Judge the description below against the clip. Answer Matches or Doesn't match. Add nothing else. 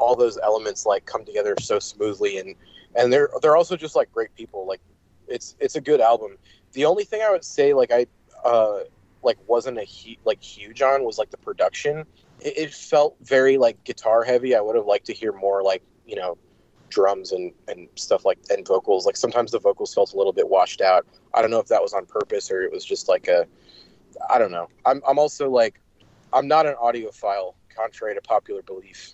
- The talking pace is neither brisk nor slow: Doesn't match